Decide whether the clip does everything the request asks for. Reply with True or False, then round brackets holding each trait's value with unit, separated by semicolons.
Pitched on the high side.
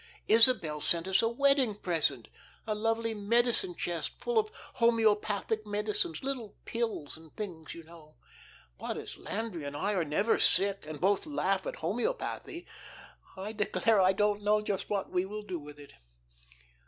True (205 Hz)